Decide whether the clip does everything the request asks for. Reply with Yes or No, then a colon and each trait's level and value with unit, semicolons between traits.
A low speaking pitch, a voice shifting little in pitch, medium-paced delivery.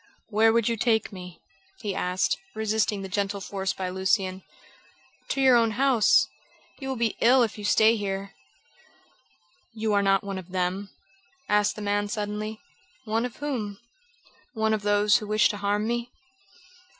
No: high, 210 Hz; narrow, 2.1 semitones; average, 165 wpm